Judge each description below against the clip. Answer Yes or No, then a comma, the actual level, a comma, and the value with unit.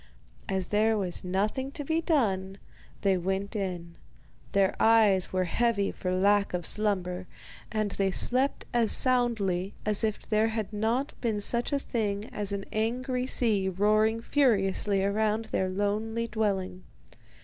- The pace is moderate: Yes, average, 145 wpm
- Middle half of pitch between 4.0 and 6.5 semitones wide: No, average, 2.9 semitones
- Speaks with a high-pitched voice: Yes, high, 210 Hz